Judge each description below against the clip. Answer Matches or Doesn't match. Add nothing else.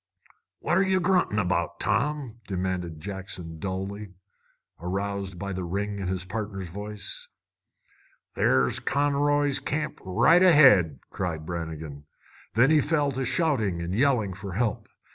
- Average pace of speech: Doesn't match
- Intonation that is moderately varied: Doesn't match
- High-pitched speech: Doesn't match